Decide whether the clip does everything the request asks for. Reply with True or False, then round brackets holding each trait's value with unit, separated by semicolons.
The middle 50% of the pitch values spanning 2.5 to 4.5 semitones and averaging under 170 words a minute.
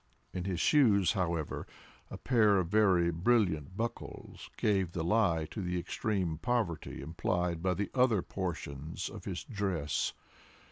True (4.0 semitones; 140 wpm)